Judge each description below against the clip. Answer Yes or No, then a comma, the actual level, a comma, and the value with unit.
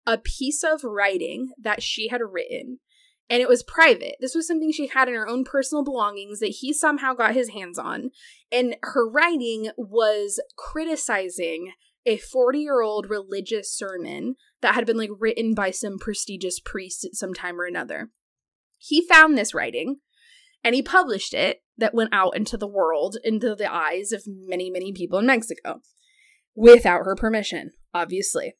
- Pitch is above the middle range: Yes, high, 230 Hz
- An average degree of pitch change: No, wide, 5.7 semitones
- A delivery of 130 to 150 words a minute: No, average, 170 wpm